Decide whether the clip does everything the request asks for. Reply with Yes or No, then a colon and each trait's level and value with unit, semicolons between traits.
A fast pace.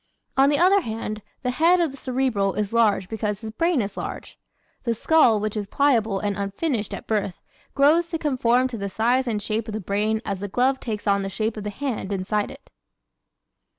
Yes: fast, 210 wpm